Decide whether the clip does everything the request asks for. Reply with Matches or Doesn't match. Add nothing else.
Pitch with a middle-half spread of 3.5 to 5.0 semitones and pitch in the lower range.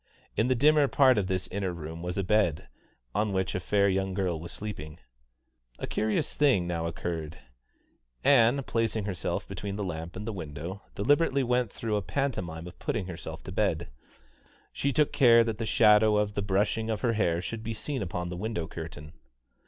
Matches